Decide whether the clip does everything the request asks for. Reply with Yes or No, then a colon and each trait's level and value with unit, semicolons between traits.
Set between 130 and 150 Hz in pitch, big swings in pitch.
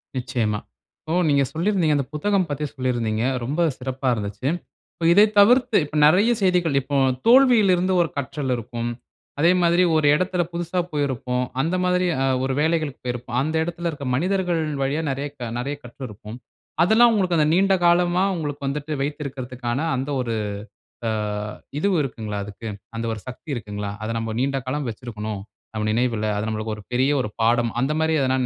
Yes: medium, 140 Hz; wide, 6.1 semitones